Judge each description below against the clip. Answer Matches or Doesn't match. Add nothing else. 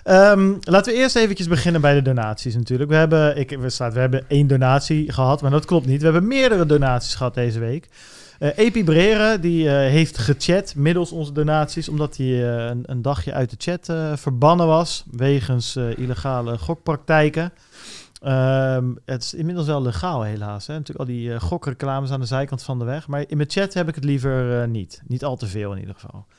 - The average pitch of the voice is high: Doesn't match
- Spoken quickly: Matches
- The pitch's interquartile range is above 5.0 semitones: Doesn't match